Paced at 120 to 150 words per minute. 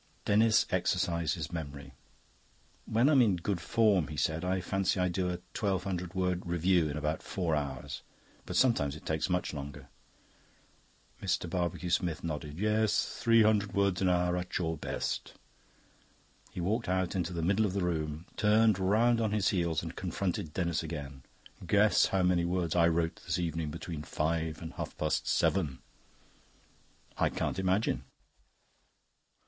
No: average, 160 wpm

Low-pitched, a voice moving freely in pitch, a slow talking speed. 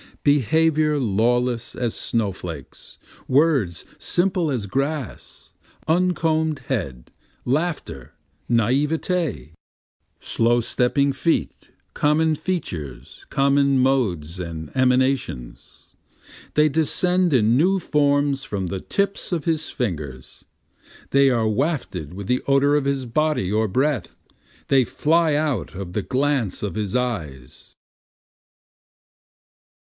Yes: low, 130 Hz; wide, 6.6 semitones; slow, 110 wpm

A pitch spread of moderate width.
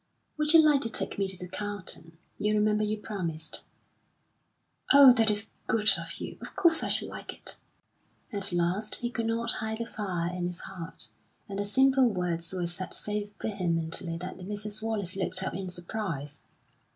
Yes: average, 3.7 semitones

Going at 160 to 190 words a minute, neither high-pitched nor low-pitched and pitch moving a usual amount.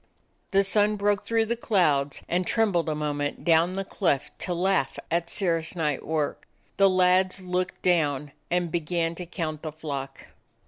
Yes: average, 175 wpm; medium, 175 Hz; average, 3.5 semitones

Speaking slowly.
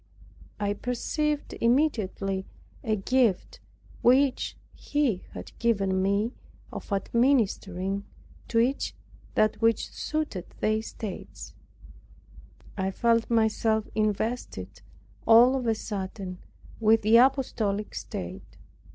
Yes: slow, 100 wpm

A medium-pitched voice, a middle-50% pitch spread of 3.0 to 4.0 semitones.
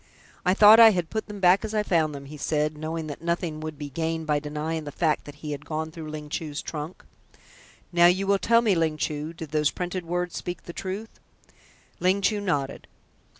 Yes: medium, 165 Hz; average, 3.3 semitones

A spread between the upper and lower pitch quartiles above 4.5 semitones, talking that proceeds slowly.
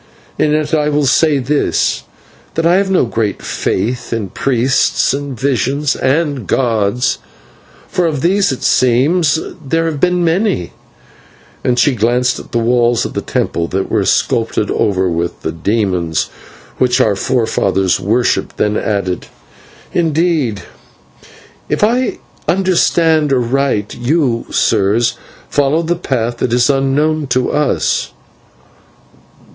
Yes: wide, 5.4 semitones; slow, 130 wpm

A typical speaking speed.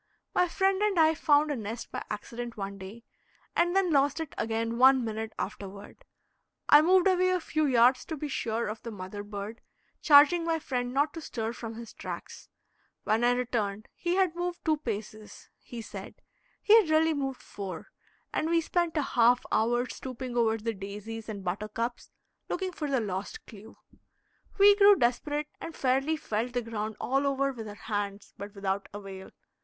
Yes: average, 180 wpm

